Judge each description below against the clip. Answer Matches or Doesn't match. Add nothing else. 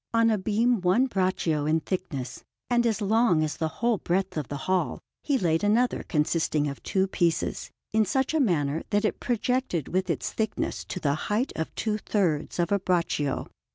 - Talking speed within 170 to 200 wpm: Matches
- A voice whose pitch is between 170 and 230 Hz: Matches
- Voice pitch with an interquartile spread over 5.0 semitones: Matches